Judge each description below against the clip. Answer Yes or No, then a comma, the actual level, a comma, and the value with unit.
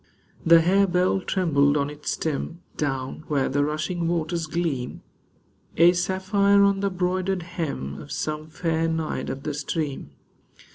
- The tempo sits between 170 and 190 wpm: No, average, 140 wpm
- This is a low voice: No, medium, 165 Hz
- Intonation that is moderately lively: Yes, average, 3.5 semitones